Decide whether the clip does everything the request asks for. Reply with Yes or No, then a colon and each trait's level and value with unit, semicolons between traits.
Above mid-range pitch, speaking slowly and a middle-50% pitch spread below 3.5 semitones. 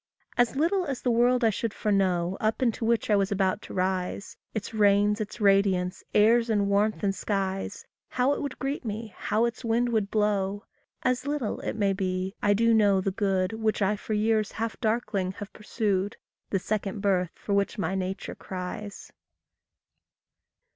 No: high, 210 Hz; average, 175 wpm; narrow, 2.6 semitones